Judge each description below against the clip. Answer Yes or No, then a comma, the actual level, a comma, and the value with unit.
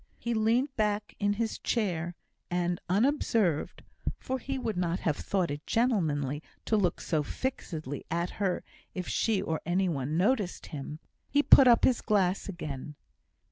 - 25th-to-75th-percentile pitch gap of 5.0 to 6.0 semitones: Yes, wide, 5.6 semitones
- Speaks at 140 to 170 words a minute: Yes, average, 155 wpm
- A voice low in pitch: No, medium, 185 Hz